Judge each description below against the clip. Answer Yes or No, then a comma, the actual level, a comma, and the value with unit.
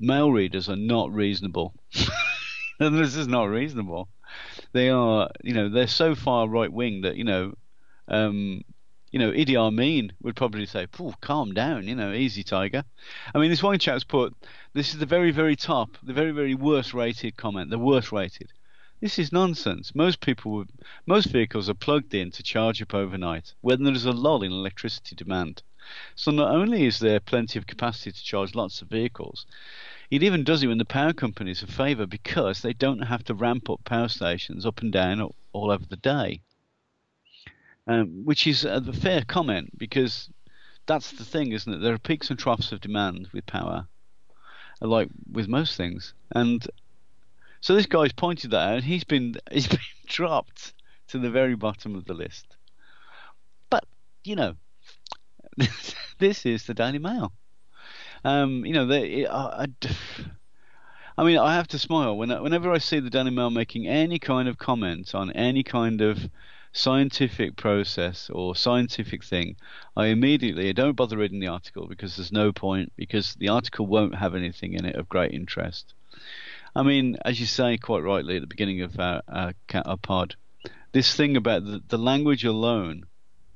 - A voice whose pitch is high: No, low, 115 Hz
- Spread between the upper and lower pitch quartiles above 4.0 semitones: Yes, average, 5.2 semitones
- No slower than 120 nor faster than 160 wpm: No, average, 175 wpm